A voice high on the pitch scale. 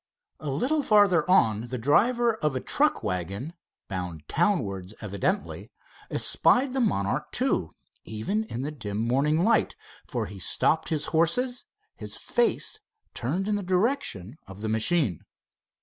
No: medium, 150 Hz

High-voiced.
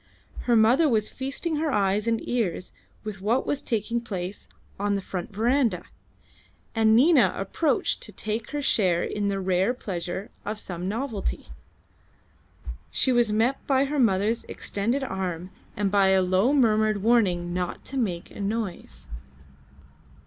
Yes: high, 215 Hz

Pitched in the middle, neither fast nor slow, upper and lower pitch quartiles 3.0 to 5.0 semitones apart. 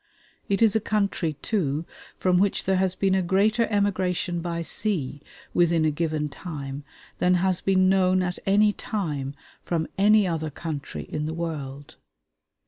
Yes: medium, 180 Hz; average, 155 wpm; average, 3.7 semitones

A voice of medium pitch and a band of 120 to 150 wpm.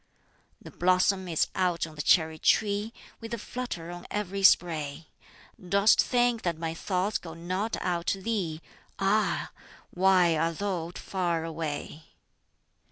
Yes: medium, 180 Hz; average, 140 wpm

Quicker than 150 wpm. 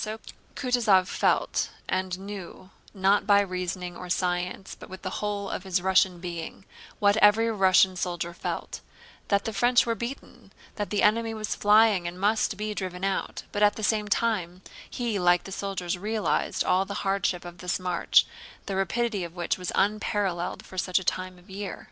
Yes: average, 175 wpm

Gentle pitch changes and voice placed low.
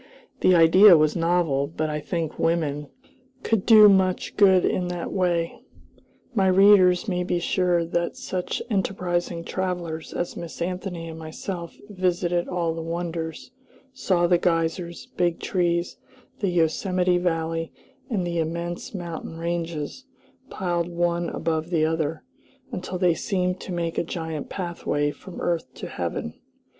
No: narrow, 1.7 semitones; medium, 175 Hz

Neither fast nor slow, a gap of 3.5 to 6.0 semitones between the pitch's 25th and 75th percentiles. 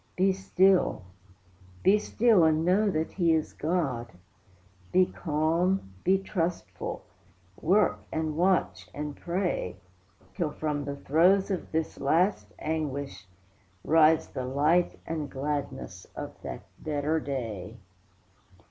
No: slow, 115 wpm; average, 4.1 semitones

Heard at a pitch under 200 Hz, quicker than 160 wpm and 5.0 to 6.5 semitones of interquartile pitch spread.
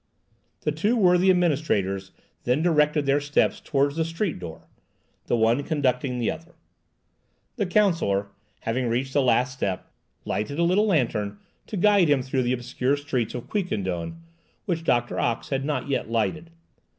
No: medium, 140 Hz; average, 155 wpm; wide, 5.6 semitones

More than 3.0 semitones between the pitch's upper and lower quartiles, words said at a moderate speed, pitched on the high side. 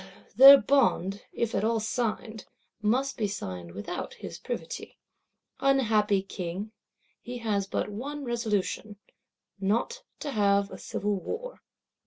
No: average, 4.1 semitones; slow, 120 wpm; high, 215 Hz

